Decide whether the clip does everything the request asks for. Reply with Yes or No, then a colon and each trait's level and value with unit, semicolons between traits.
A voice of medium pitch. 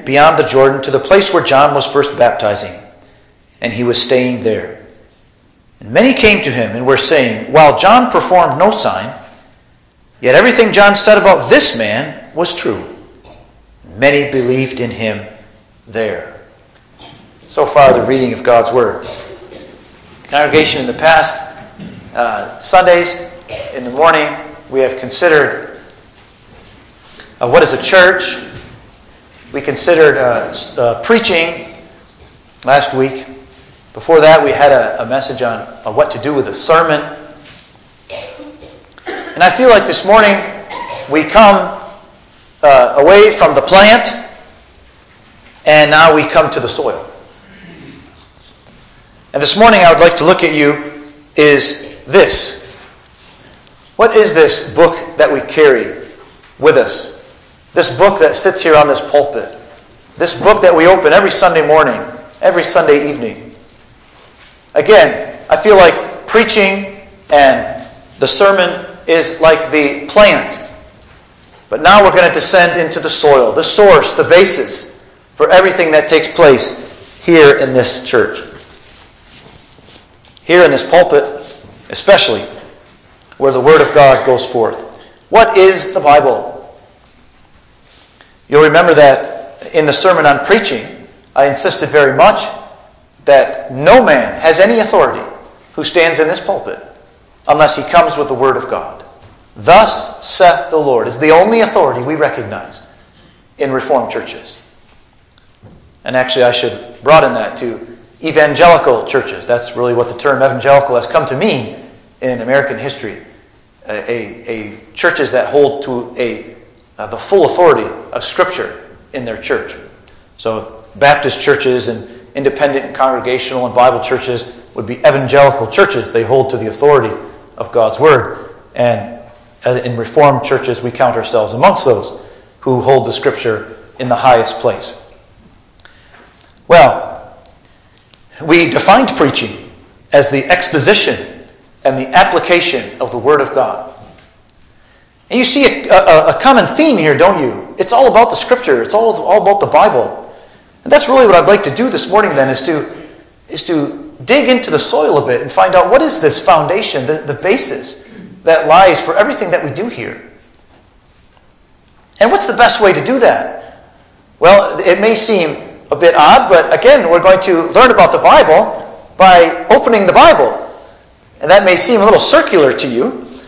Yes: medium, 155 Hz